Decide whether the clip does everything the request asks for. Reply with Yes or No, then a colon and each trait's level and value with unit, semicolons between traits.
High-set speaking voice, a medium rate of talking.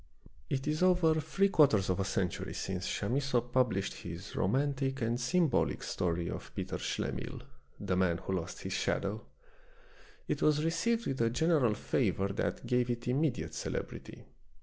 No: low, 125 Hz; average, 150 wpm